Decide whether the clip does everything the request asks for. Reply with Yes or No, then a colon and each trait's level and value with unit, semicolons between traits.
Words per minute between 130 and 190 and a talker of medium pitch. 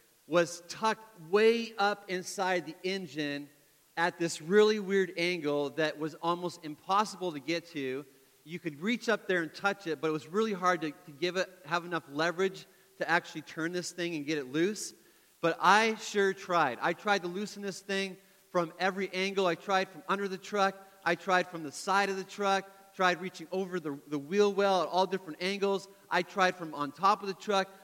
No: fast, 205 wpm; medium, 180 Hz